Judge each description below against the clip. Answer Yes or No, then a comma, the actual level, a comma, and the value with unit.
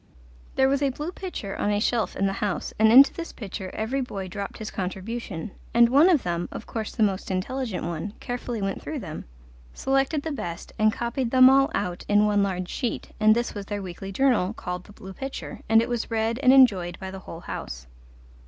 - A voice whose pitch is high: Yes, high, 215 Hz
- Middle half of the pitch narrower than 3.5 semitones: No, average, 5.0 semitones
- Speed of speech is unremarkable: No, fast, 215 wpm